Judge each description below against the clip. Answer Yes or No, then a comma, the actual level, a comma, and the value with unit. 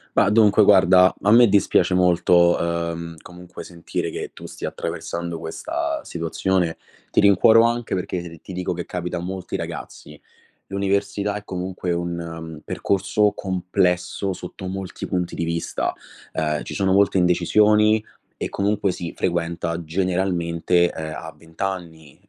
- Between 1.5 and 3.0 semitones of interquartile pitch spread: Yes, narrow, 2.5 semitones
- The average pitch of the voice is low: Yes, very low, 90 Hz